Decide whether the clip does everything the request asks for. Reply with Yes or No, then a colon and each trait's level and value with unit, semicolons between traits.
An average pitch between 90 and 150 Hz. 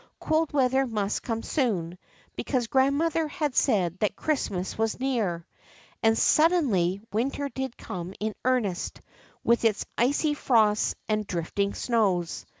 No: high, 230 Hz